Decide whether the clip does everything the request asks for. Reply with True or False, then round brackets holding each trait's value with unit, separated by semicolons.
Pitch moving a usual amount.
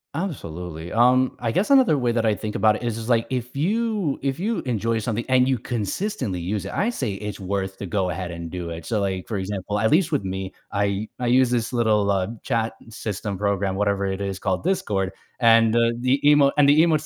True (4.9 semitones)